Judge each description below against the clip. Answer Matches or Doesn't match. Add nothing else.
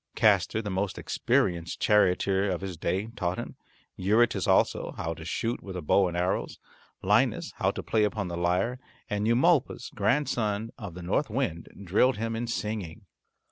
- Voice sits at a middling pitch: Doesn't match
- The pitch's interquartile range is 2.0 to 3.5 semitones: Doesn't match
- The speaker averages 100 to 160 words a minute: Doesn't match